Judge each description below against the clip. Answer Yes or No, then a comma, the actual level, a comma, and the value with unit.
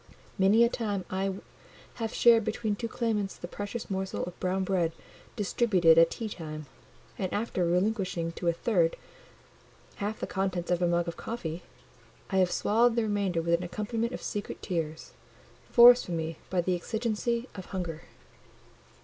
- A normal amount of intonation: Yes, average, 4.2 semitones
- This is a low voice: No, high, 190 Hz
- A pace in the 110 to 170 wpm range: Yes, average, 165 wpm